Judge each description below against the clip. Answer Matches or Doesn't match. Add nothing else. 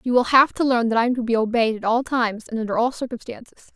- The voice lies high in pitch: Matches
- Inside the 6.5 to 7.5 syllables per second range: Matches